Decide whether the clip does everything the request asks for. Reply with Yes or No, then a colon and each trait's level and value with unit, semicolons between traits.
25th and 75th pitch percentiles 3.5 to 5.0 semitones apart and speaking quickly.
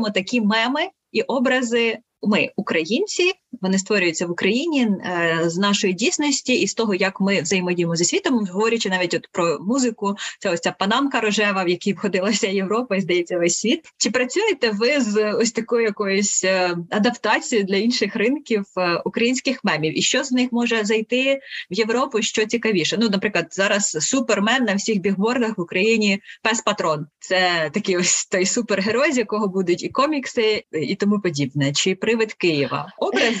Yes: average, 3.9 semitones; fast, 165 wpm